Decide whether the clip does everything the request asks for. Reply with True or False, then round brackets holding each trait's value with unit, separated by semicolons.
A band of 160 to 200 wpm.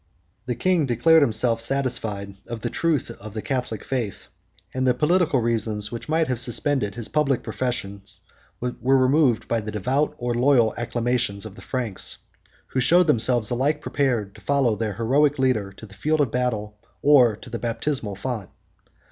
True (170 wpm)